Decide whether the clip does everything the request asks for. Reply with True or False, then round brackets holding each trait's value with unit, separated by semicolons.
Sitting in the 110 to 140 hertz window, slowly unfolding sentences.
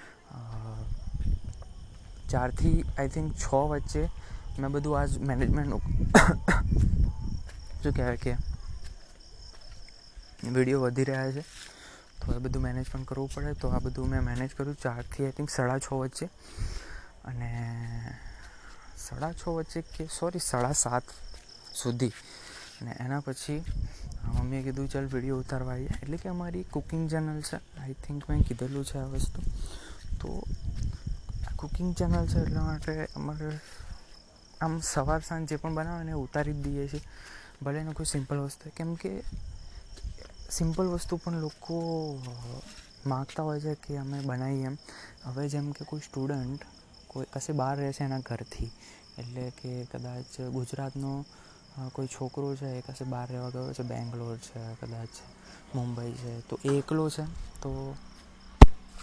False (135 Hz; 135 wpm)